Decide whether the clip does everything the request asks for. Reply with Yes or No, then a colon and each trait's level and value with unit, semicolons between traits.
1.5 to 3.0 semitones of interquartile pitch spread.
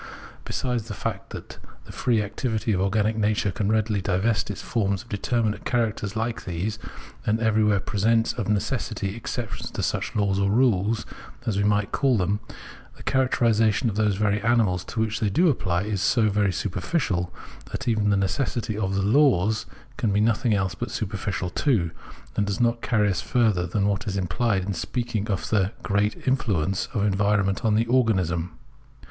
Yes: average, 2.7 semitones